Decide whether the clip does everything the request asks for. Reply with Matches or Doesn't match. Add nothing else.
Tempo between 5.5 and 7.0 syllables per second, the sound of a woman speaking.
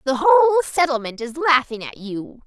Matches